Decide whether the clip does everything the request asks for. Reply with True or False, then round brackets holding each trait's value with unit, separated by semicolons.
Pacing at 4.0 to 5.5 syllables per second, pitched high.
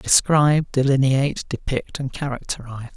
False (5.3 syllables/s; 135 Hz)